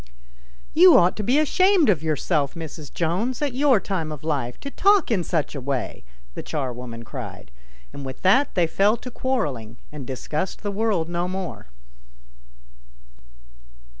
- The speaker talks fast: No, average, 155 wpm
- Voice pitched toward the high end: No, medium, 175 Hz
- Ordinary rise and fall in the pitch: No, wide, 8.7 semitones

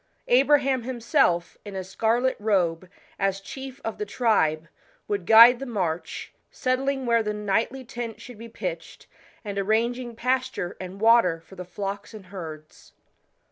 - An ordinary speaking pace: Yes, average, 145 wpm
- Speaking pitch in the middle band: No, high, 220 Hz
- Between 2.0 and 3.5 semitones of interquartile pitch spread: No, average, 4.3 semitones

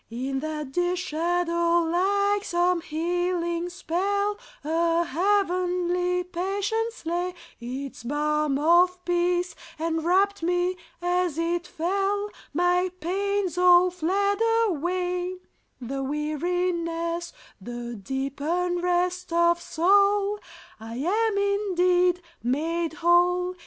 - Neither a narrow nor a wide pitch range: No, narrow, 1.8 semitones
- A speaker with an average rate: No, slow, 95 wpm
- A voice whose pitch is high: Yes, very high, 350 Hz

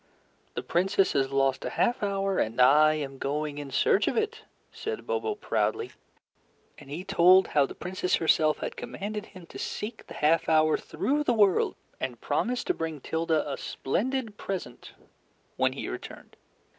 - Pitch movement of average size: No, wide, 6.0 semitones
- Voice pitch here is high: No, medium, 175 Hz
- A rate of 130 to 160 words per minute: No, average, 170 wpm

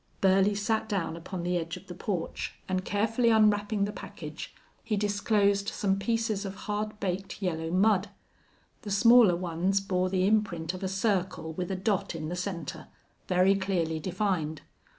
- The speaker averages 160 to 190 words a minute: Yes, average, 165 wpm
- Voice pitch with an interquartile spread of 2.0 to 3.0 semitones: Yes, narrow, 2.6 semitones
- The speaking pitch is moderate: No, high, 195 Hz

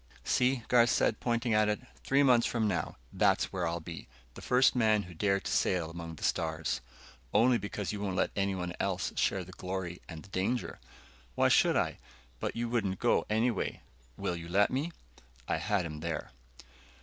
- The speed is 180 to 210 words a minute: Yes, average, 185 wpm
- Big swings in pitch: No, average, 4.9 semitones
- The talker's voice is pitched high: No, low, 100 Hz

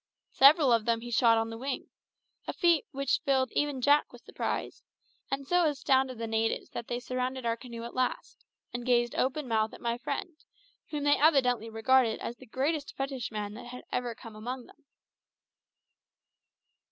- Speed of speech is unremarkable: Yes, average, 175 wpm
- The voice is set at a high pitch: Yes, very high, 250 Hz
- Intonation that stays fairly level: No, average, 3.0 semitones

